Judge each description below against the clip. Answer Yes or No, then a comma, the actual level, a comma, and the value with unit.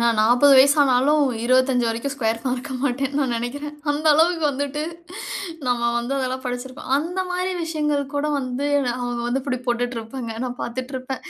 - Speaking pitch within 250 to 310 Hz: Yes, very high, 260 Hz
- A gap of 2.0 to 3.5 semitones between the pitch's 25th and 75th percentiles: Yes, average, 2.8 semitones